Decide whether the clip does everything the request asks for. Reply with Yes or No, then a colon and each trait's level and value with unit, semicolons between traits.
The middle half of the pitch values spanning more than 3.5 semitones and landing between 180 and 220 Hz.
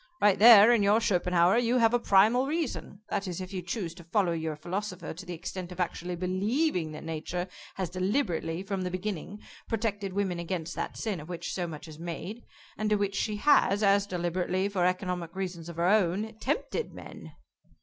No: average, 3.1 semitones; medium, 185 Hz